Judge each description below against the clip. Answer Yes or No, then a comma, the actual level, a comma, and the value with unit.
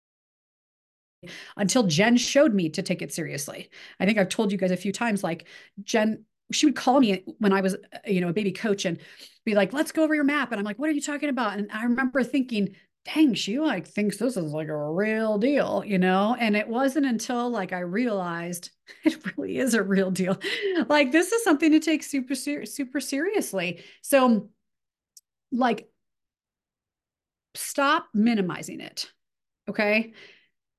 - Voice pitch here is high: Yes, high, 220 Hz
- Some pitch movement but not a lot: No, wide, 6.3 semitones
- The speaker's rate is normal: Yes, average, 180 wpm